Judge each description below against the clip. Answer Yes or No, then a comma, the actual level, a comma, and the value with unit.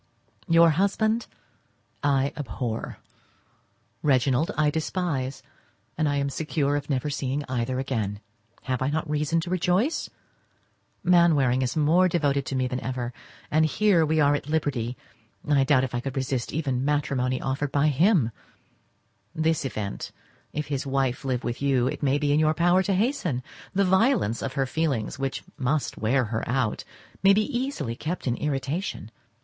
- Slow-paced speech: No, average, 160 wpm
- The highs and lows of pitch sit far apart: No, average, 3.7 semitones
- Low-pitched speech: No, medium, 145 Hz